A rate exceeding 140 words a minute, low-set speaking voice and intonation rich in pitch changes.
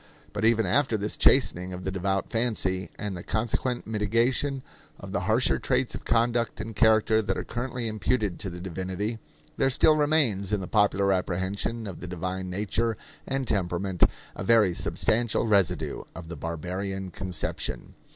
No: average, 160 wpm; low, 105 Hz; average, 3.9 semitones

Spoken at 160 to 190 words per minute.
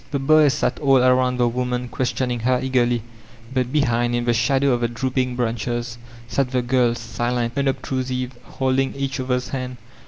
Yes: average, 165 wpm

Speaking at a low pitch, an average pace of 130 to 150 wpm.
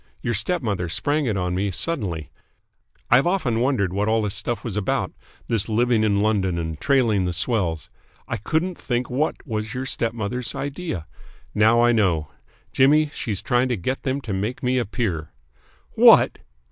No: low, 115 Hz; average, 170 wpm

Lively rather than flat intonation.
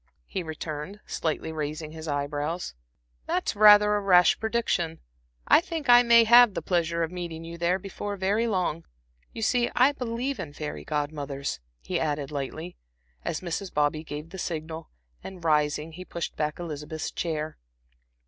No: average, 4.9 semitones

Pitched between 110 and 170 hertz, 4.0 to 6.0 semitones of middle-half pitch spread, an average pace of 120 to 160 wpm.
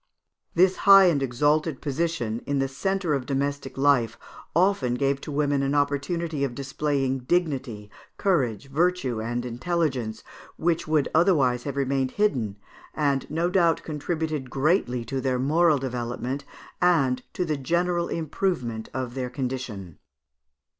Yes: medium, 140 Hz; average, 4.5 semitones; slow, 135 wpm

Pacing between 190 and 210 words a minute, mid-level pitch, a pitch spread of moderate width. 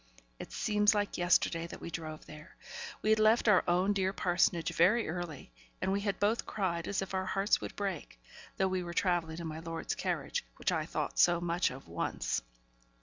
Yes: average, 200 wpm; medium, 180 Hz; average, 3.1 semitones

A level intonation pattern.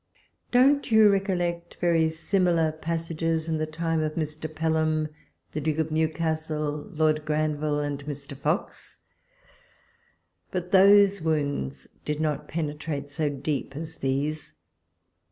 Yes: narrow, 1.7 semitones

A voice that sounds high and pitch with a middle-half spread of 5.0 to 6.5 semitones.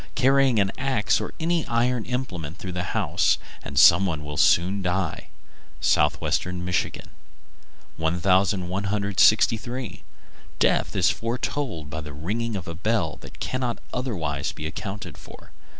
No: very low, 95 Hz; wide, 5.6 semitones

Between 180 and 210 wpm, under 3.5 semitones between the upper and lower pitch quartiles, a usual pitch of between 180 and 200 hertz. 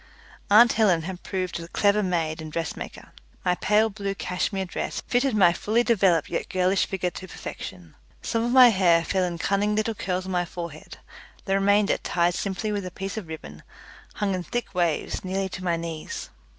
Yes: average, 190 wpm; average, 3.0 semitones; medium, 185 Hz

